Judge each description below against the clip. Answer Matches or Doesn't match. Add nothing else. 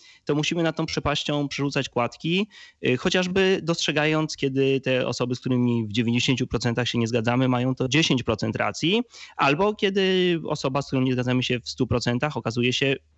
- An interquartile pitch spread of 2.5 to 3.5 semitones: Doesn't match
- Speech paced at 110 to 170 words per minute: Matches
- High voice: Doesn't match